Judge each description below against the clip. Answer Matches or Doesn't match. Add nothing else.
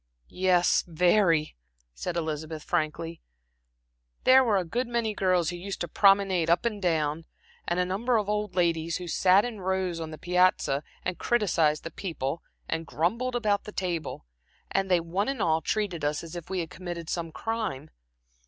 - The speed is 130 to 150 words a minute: Doesn't match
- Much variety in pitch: Doesn't match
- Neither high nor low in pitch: Matches